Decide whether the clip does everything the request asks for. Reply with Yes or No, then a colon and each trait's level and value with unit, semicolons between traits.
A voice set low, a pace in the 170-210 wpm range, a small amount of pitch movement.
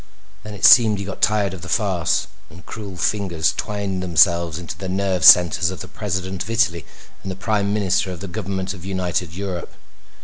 Yes: very low, 95 Hz; average, 195 wpm; narrow, 2.3 semitones